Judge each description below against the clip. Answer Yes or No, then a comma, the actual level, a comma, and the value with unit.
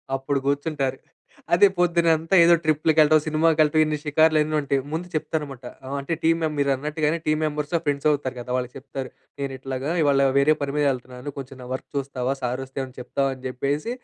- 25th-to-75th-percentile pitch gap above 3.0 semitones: No, narrow, 2.6 semitones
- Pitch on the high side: No, medium, 145 Hz